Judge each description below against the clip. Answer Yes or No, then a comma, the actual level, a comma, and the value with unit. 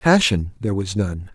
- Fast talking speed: No, average, 180 wpm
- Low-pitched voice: Yes, low, 105 Hz